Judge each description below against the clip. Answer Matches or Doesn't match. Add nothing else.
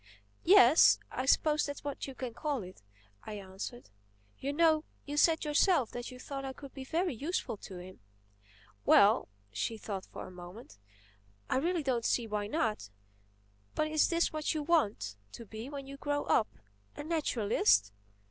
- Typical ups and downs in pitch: Doesn't match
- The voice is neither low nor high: Doesn't match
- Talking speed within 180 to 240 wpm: Doesn't match